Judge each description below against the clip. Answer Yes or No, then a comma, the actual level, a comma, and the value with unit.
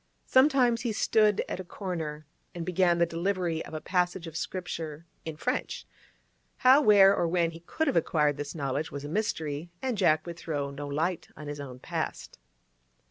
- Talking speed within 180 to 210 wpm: Yes, average, 185 wpm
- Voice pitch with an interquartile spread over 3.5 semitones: Yes, average, 4.2 semitones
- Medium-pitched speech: Yes, medium, 170 Hz